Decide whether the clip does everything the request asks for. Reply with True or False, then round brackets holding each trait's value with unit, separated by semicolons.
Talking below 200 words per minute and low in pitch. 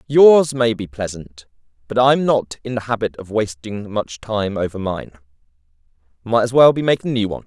True (185 wpm; 110 Hz)